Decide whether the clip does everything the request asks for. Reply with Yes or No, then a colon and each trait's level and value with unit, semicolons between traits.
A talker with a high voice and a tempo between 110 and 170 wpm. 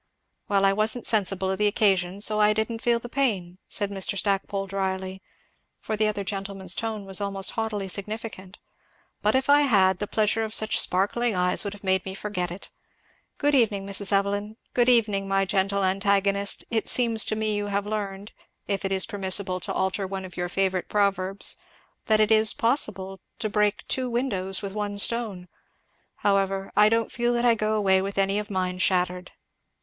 No: high, 200 Hz; average, 185 wpm